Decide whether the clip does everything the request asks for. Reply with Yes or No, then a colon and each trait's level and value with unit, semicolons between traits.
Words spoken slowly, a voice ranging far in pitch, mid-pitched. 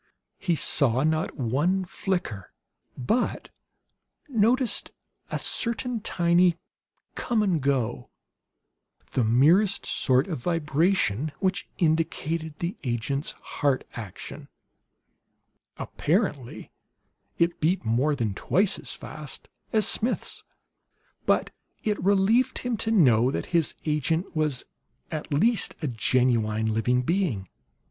Yes: slow, 110 wpm; wide, 7.2 semitones; medium, 160 Hz